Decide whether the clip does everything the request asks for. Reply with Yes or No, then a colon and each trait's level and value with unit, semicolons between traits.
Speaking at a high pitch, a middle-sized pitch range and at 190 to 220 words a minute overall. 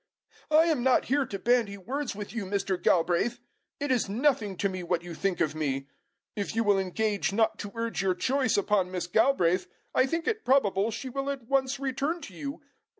No: high, 220 Hz; wide, 5.9 semitones; fast, 205 wpm